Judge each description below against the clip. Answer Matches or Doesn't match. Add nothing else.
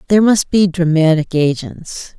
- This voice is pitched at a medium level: Matches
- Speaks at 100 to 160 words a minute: Matches